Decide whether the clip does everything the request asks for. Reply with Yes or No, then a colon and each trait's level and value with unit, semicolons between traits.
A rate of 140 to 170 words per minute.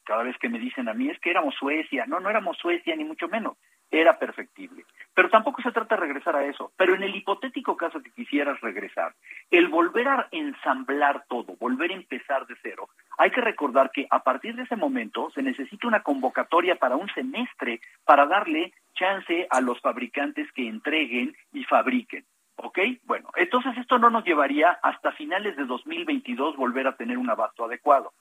No: fast, 190 wpm